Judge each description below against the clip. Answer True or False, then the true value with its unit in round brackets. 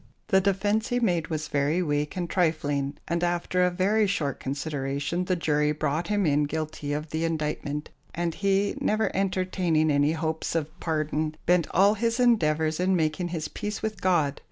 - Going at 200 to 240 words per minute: False (175 wpm)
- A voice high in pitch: False (165 Hz)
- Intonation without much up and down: False (3.6 semitones)